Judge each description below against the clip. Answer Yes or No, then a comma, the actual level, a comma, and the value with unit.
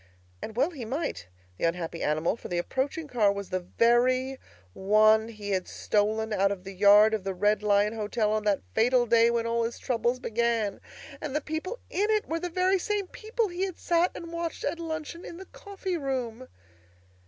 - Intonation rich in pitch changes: Yes, wide, 7.8 semitones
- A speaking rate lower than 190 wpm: No, average, 200 wpm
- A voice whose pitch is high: Yes, high, 235 Hz